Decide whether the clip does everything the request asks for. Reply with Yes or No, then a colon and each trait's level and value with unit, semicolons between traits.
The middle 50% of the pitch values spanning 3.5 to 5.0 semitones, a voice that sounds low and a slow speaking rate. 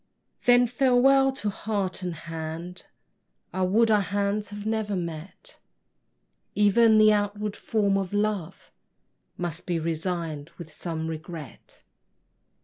No: average, 4.1 semitones; high, 200 Hz; slow, 120 wpm